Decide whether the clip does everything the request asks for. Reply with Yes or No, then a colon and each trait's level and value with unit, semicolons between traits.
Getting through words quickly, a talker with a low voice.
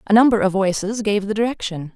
No: fast, 215 wpm; high, 205 Hz